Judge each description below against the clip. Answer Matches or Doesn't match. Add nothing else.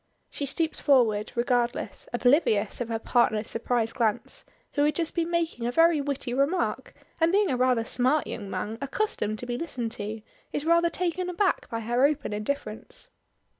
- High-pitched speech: Matches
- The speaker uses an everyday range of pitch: Doesn't match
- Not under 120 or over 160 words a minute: Doesn't match